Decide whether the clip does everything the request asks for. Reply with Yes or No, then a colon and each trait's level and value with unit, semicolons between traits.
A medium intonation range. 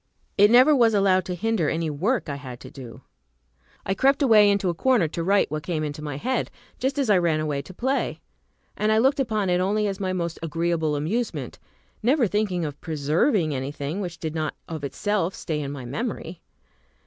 No: wide, 5.8 semitones